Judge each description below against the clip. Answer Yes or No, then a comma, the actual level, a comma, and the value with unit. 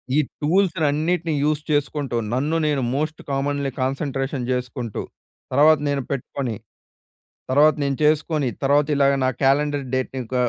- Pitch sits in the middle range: Yes, medium, 145 Hz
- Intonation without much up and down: Yes, narrow, 2.2 semitones